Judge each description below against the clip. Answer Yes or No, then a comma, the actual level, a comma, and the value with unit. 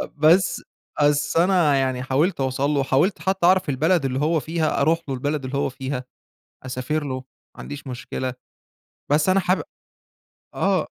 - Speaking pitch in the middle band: Yes, medium, 145 Hz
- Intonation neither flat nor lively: Yes, average, 3.8 semitones